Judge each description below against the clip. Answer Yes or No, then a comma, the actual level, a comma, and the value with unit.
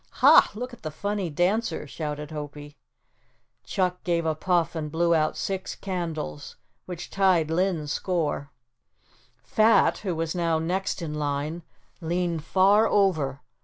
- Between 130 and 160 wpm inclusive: Yes, slow, 135 wpm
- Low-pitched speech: No, medium, 170 Hz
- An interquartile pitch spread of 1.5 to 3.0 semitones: No, average, 3.5 semitones